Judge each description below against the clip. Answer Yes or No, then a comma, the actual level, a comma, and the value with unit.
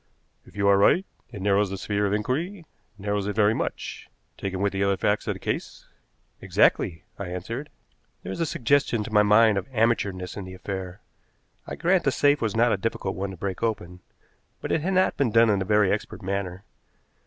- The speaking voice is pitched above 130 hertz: No, low, 105 Hz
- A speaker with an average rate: No, fast, 210 wpm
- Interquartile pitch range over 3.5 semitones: No, average, 3.0 semitones